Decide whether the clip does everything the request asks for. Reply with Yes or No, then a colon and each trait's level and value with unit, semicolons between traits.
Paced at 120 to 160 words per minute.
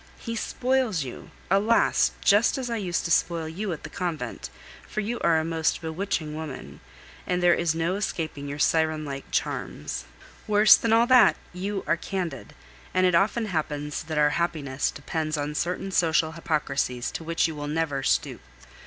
No: average, 170 wpm